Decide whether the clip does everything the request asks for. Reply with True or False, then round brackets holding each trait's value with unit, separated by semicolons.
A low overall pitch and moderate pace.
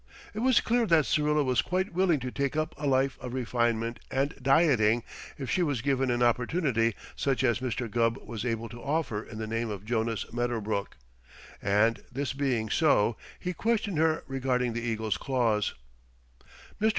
True (125 Hz; 175 wpm)